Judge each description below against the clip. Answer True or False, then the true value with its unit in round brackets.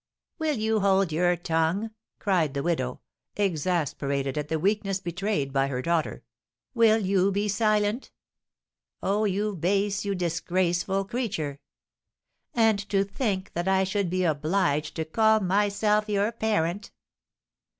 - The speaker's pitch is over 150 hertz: True (190 Hz)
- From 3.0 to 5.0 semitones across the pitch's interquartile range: True (4.2 semitones)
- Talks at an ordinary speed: False (130 wpm)